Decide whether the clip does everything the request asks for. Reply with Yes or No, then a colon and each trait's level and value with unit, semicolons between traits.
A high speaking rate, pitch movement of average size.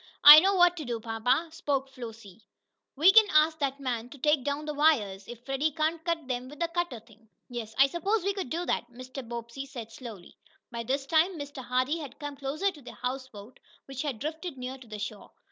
Yes: fast, 215 wpm; average, 4.6 semitones